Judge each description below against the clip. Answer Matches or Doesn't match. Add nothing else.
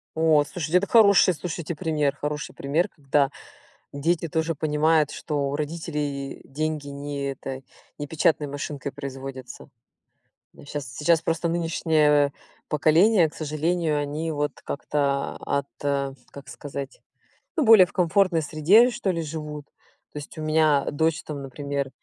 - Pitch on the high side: Doesn't match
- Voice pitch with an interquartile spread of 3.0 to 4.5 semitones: Doesn't match